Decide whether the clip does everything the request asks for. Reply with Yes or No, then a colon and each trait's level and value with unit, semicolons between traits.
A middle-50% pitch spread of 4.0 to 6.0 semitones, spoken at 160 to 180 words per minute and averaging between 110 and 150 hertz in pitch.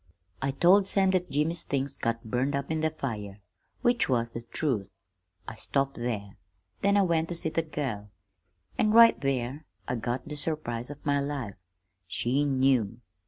Yes: average, 5.0 semitones; average, 170 wpm; medium, 140 Hz